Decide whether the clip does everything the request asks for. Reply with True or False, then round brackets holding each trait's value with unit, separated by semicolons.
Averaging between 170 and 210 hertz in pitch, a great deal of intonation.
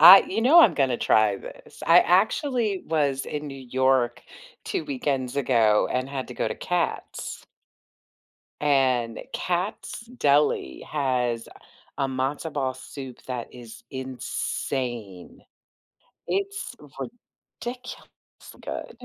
False (135 Hz; 6.0 semitones)